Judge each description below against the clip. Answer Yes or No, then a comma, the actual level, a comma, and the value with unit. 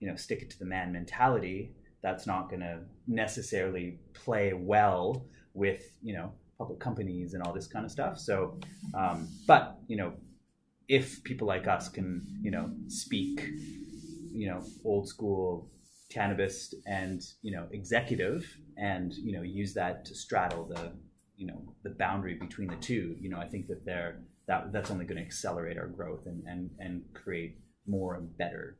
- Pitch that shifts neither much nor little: Yes, average, 3.0 semitones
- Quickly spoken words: No, average, 175 wpm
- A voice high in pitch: No, very low, 95 Hz